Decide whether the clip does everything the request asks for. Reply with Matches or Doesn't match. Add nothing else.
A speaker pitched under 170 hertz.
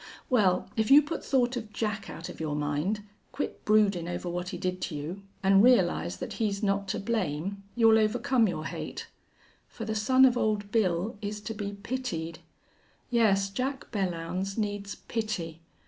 Doesn't match